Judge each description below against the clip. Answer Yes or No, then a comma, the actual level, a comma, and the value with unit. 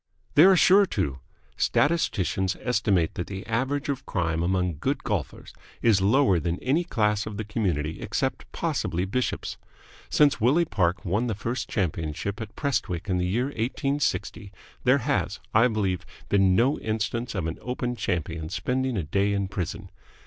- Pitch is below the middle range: Yes, low, 105 Hz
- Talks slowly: No, average, 165 wpm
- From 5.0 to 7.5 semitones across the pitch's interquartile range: Yes, wide, 5.4 semitones